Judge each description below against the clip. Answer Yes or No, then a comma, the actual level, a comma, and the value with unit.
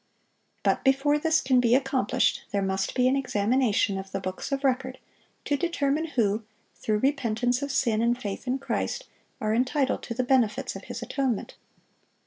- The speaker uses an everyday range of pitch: Yes, average, 4.1 semitones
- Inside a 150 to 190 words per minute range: Yes, average, 170 wpm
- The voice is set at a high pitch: Yes, very high, 255 Hz